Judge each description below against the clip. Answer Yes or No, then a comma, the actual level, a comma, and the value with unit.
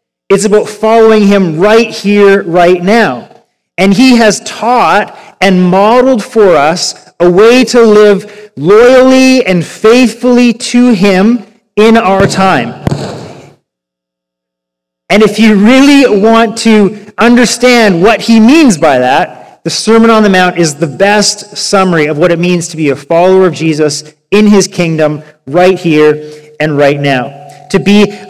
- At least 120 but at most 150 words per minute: Yes, average, 145 wpm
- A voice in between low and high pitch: No, high, 200 Hz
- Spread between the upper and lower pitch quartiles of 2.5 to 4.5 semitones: No, average, 4.9 semitones